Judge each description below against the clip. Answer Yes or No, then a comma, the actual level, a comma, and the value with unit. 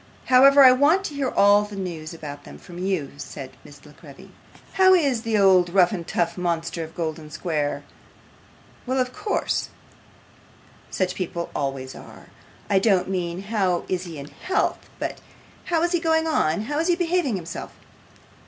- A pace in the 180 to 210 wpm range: No, average, 170 wpm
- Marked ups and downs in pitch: Yes, wide, 8.3 semitones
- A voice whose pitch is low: No, high, 190 Hz